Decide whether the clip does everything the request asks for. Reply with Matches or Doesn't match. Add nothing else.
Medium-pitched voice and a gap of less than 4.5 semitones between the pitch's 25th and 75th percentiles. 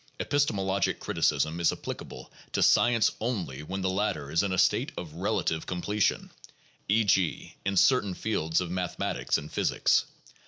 Doesn't match